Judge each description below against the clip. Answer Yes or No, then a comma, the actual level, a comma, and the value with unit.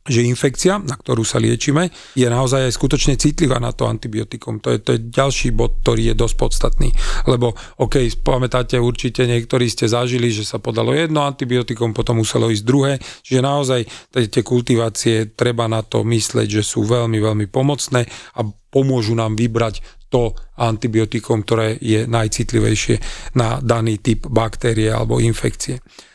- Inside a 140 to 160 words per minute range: Yes, average, 155 wpm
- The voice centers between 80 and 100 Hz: No, low, 120 Hz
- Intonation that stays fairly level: Yes, narrow, 2.2 semitones